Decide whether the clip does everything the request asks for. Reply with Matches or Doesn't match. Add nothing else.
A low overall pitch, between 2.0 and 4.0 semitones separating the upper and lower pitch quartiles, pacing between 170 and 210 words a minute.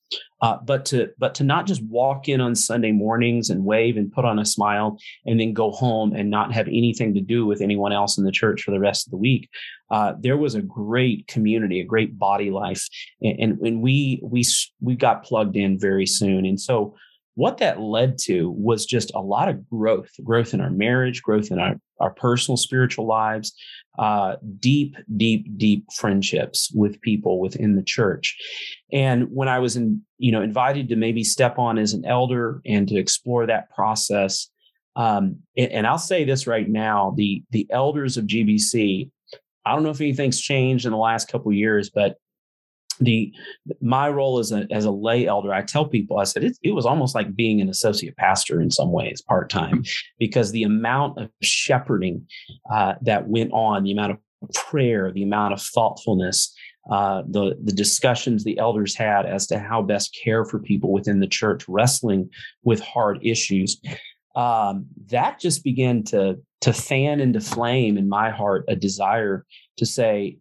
Matches